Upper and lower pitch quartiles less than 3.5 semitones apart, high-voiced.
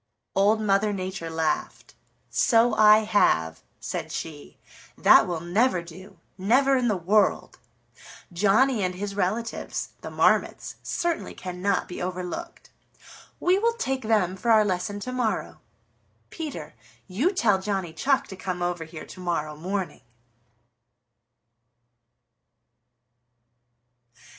No: average, 4.2 semitones; high, 200 Hz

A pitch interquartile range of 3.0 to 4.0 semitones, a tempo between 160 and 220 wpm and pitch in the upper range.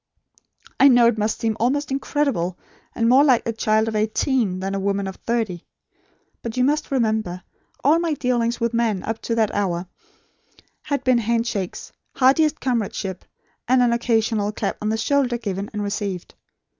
Yes: average, 3.6 semitones; average, 170 wpm; high, 230 Hz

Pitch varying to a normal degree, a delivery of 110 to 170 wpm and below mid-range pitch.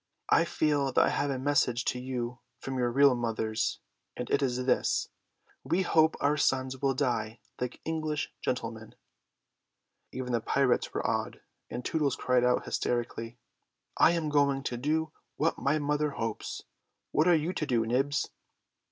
Yes: average, 3.4 semitones; average, 160 wpm; low, 130 Hz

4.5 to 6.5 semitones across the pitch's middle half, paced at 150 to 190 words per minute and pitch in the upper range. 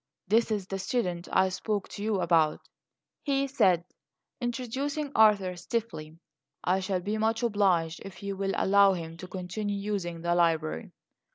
No: average, 3.8 semitones; average, 155 wpm; high, 195 Hz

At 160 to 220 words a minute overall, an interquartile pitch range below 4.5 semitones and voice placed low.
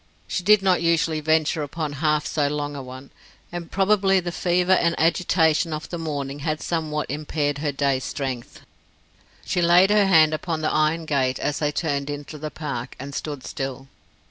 No: average, 180 wpm; average, 2.8 semitones; medium, 155 Hz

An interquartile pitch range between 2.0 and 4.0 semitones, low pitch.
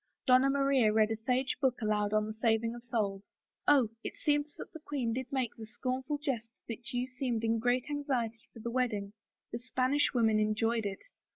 No: average, 2.9 semitones; high, 240 Hz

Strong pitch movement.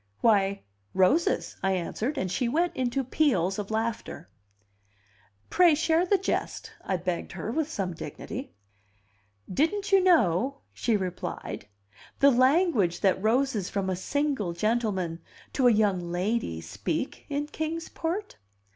Yes: wide, 8.0 semitones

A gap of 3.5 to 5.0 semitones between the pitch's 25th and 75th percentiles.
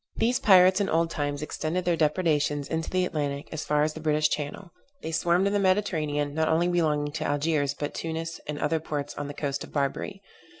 No: average, 2.9 semitones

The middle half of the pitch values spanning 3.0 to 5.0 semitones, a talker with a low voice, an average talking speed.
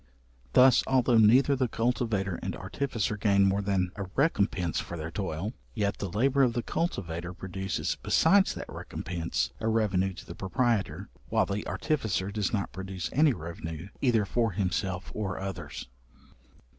Yes: average, 4.2 semitones; low, 100 Hz; average, 155 wpm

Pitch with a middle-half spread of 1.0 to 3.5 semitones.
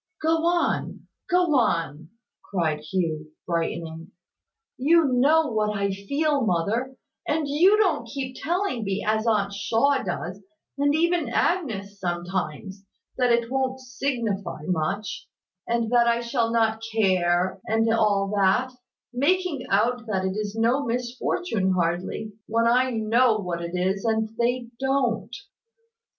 No: average, 5.3 semitones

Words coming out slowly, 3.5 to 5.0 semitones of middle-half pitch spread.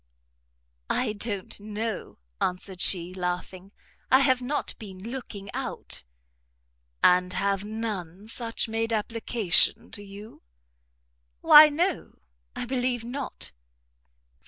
Yes: slow, 105 wpm; average, 4.1 semitones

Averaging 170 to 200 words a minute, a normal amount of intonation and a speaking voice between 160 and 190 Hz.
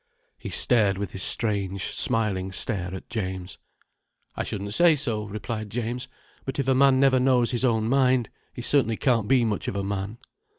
No: average, 180 wpm; average, 4.2 semitones; low, 115 Hz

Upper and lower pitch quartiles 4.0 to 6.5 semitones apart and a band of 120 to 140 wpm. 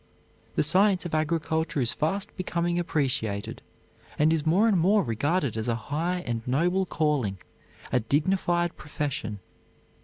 Yes: average, 5.1 semitones; slow, 135 wpm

